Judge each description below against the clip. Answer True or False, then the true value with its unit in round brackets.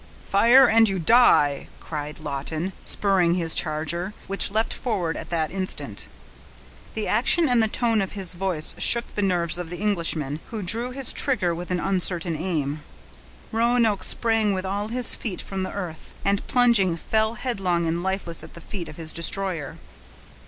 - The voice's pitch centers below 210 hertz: True (190 Hz)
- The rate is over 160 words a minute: True (170 wpm)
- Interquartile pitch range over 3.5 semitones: True (4.6 semitones)